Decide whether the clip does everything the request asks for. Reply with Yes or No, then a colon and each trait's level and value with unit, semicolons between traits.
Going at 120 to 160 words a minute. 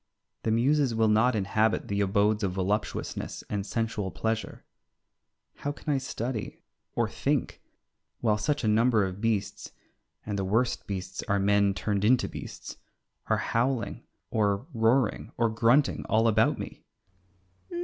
Yes: average, 140 wpm